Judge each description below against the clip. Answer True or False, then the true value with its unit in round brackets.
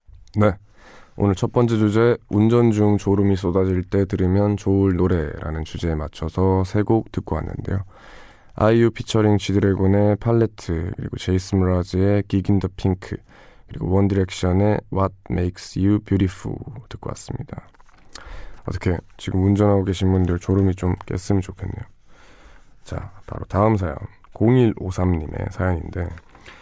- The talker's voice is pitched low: True (95 Hz)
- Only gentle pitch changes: True (2.3 semitones)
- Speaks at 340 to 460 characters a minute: False (320 characters per minute)